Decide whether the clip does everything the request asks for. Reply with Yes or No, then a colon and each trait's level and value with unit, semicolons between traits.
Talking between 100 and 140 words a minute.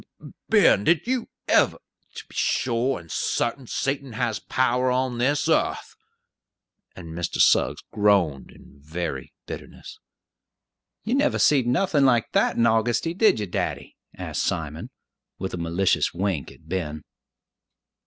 Yes: slow, 135 wpm